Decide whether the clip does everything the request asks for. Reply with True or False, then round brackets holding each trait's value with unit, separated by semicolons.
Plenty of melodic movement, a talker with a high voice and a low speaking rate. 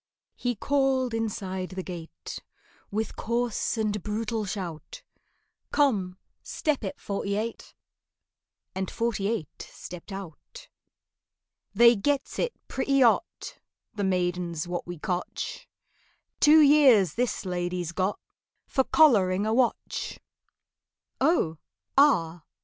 True (5.7 semitones; 210 Hz; 110 wpm)